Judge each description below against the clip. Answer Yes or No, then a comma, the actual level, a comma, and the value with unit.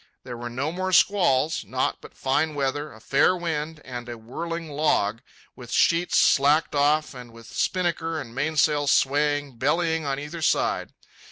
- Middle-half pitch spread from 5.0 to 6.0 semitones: No, average, 3.7 semitones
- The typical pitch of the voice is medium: Yes, medium, 145 Hz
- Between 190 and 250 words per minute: No, average, 165 wpm